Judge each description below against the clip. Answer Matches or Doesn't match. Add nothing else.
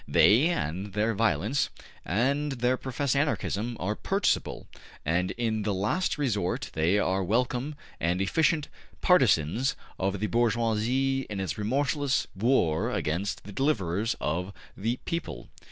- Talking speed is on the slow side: Matches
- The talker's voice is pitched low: Matches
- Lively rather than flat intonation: Matches